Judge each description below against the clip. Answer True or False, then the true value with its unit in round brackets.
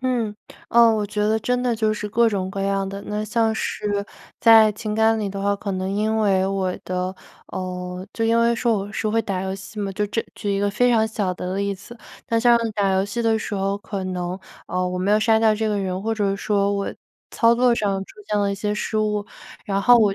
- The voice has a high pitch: True (205 Hz)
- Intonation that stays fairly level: True (2.2 semitones)